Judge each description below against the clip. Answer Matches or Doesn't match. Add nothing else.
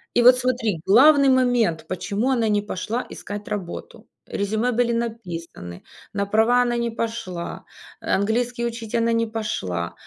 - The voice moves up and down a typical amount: Matches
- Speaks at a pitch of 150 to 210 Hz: Doesn't match